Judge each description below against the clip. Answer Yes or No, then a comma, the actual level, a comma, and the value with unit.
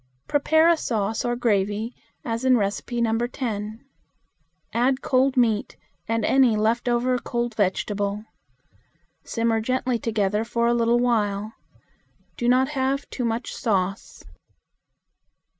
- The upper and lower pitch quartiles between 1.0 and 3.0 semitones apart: Yes, average, 2.7 semitones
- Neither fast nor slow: No, slow, 120 wpm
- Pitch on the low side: No, high, 235 Hz